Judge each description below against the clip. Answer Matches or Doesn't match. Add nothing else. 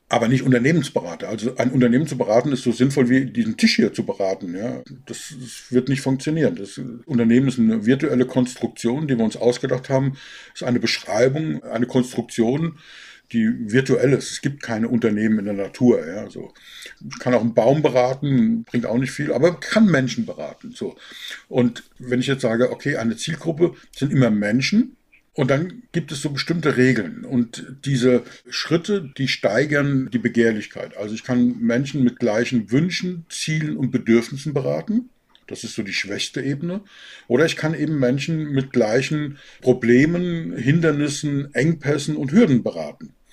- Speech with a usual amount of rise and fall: Matches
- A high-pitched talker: Doesn't match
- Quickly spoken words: Doesn't match